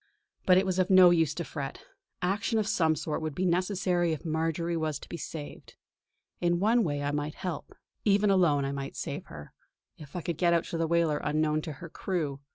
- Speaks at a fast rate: Yes, fast, 215 wpm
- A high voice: No, medium, 165 Hz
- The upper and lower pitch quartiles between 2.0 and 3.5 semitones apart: Yes, average, 3.1 semitones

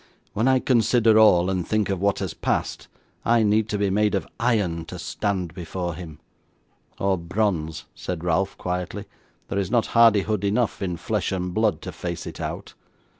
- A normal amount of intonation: Yes, average, 3.4 semitones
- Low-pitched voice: Yes, low, 100 Hz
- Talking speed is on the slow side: No, average, 175 wpm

